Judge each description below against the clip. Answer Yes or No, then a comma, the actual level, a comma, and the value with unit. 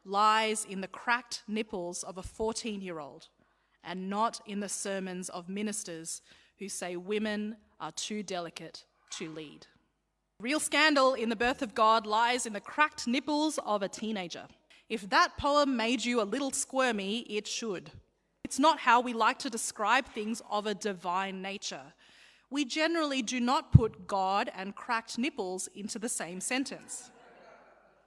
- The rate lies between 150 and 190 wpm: Yes, average, 160 wpm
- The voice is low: No, high, 220 Hz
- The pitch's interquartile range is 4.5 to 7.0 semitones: Yes, average, 4.8 semitones